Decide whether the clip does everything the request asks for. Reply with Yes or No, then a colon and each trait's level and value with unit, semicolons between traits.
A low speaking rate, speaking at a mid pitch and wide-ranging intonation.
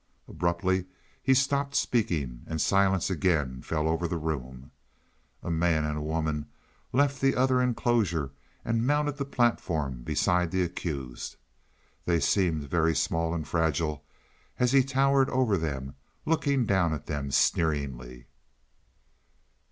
No: slow, 130 wpm; very low, 85 Hz; wide, 7.9 semitones